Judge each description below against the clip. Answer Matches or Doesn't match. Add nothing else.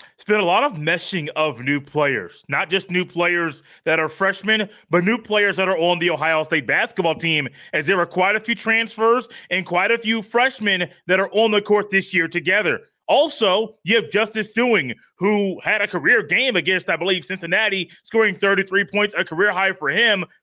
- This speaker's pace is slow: Doesn't match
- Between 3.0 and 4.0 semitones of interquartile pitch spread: Matches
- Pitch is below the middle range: Doesn't match